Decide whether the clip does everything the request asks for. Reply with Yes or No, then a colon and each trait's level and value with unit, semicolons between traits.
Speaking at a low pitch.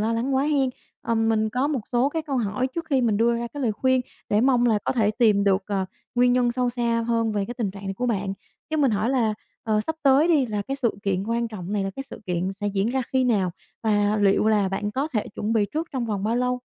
No: high, 230 Hz